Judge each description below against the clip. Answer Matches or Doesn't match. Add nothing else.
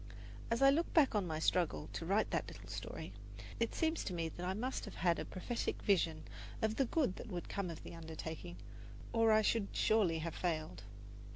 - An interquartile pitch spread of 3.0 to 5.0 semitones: Doesn't match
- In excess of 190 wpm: Matches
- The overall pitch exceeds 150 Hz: Matches